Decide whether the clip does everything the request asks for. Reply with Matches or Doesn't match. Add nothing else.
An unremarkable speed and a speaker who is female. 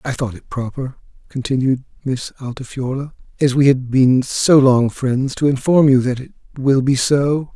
Doesn't match